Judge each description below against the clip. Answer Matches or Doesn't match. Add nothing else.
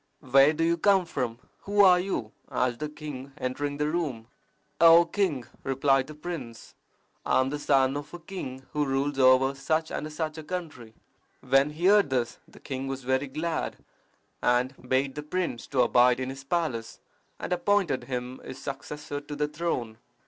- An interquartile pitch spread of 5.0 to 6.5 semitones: Doesn't match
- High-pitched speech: Doesn't match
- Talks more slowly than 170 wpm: Doesn't match